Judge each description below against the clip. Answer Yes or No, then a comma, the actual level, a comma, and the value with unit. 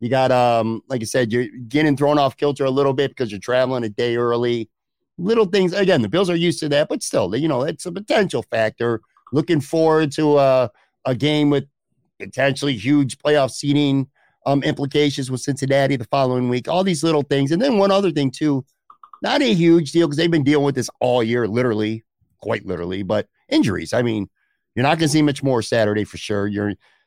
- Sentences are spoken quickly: Yes, fast, 210 wpm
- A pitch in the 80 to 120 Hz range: No, low, 135 Hz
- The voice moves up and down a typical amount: Yes, average, 4.1 semitones